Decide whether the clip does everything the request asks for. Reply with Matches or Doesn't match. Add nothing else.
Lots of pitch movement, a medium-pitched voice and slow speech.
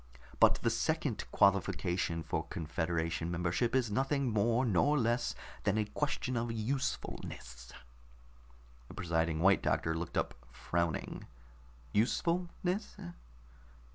Doesn't match